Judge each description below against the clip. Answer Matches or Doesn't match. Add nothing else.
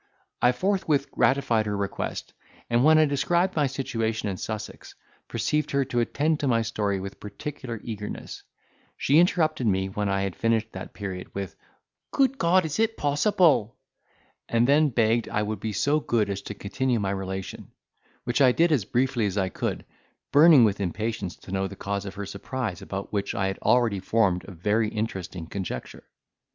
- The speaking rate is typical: Matches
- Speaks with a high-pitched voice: Doesn't match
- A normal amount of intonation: Doesn't match